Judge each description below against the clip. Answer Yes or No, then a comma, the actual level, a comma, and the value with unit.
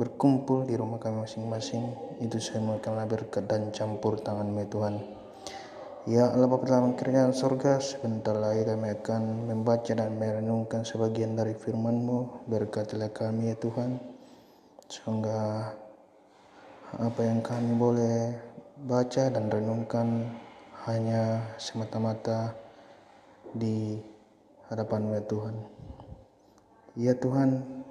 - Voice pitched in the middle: No, low, 115 Hz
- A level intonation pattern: Yes, narrow, 1.5 semitones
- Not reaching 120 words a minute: Yes, average, 110 wpm